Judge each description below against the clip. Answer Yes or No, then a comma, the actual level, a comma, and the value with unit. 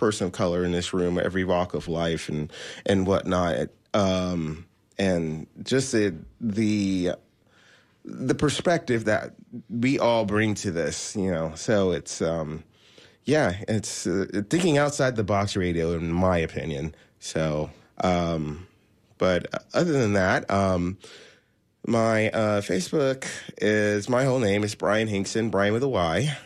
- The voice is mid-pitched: No, low, 100 Hz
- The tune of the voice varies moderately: Yes, average, 4.2 semitones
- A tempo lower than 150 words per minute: Yes, average, 140 wpm